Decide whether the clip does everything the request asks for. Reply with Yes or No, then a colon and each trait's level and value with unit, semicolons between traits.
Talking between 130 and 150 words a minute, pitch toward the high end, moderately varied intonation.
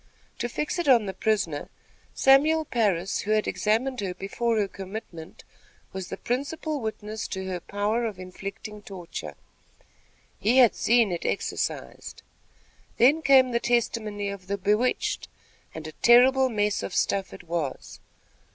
Yes: average, 145 wpm; high, 215 Hz; average, 4.0 semitones